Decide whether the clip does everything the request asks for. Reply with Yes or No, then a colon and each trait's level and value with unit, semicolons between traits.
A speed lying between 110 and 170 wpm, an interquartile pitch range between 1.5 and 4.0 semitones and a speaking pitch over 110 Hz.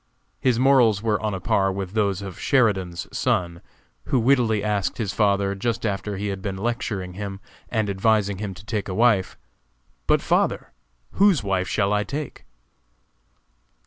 No: average, 160 wpm; average, 2.7 semitones; low, 105 Hz